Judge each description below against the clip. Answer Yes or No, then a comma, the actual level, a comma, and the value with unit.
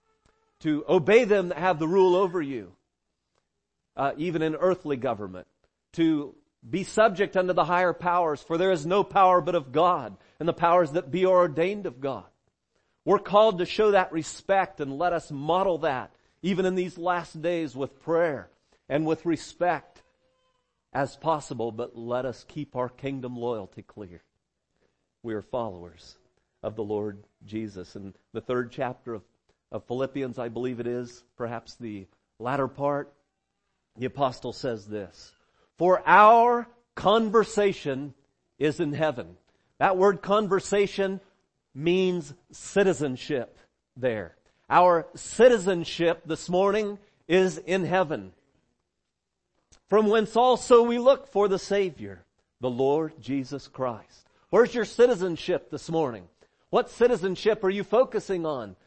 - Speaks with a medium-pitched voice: Yes, medium, 165 Hz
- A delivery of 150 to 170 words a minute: No, average, 140 wpm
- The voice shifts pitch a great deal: Yes, wide, 7.0 semitones